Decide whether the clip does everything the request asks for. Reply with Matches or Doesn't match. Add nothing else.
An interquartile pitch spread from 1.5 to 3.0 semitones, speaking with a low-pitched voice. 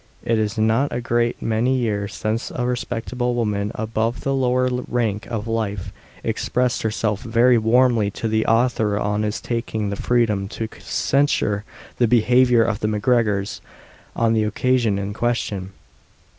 Matches